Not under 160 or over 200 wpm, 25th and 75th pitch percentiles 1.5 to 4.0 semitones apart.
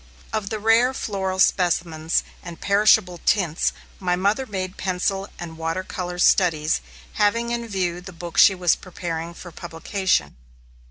No: average, 145 wpm; average, 2.8 semitones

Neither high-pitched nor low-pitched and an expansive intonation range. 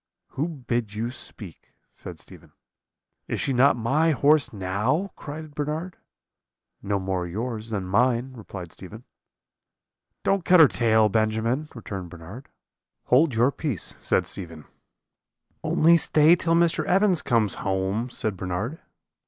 No: low, 120 Hz; wide, 6.7 semitones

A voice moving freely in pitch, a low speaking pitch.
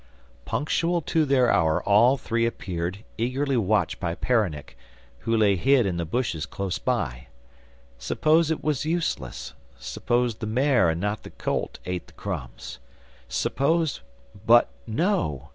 Yes: wide, 7.4 semitones; low, 115 Hz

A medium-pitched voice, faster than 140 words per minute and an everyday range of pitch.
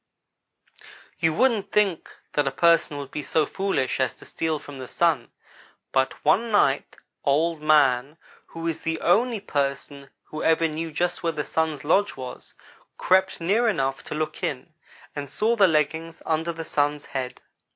Yes: medium, 155 Hz; average, 165 wpm; average, 3.1 semitones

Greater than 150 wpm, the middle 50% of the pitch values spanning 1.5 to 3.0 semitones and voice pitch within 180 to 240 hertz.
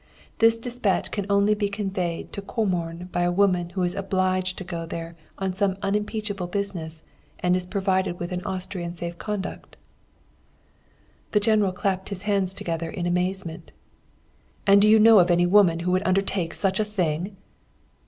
Yes: average, 165 wpm; narrow, 2.4 semitones; high, 190 Hz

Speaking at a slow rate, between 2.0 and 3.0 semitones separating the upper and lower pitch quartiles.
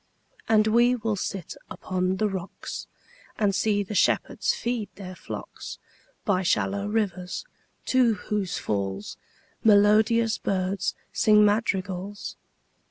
Yes: slow, 115 wpm; average, 2.7 semitones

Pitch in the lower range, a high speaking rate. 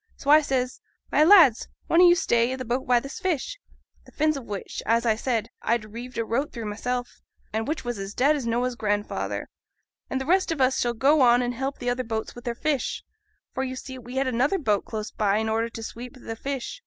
No: very high, 250 Hz; fast, 240 wpm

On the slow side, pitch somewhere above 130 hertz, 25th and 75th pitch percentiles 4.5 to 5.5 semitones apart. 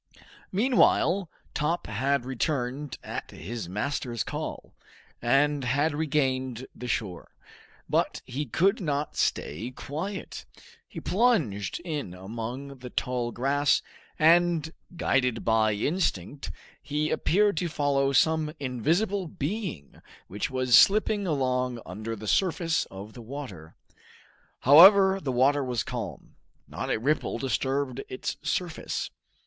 Yes: slow, 120 wpm; medium, 140 Hz; average, 4.9 semitones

